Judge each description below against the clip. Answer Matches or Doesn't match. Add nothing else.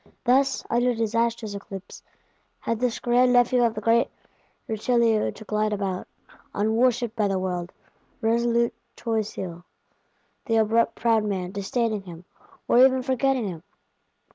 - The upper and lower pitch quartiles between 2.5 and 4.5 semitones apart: Matches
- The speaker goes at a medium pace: Doesn't match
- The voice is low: Doesn't match